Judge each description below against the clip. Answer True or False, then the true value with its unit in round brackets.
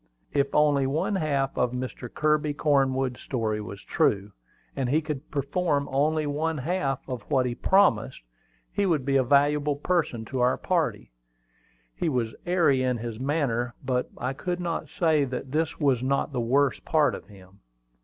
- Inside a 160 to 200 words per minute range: True (170 wpm)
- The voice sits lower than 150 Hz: True (140 Hz)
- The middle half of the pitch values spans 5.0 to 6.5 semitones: False (3.4 semitones)